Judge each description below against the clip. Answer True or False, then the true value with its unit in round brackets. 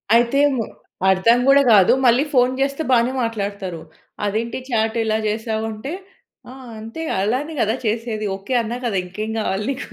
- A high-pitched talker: True (225 Hz)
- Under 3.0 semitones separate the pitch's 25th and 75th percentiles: True (2.6 semitones)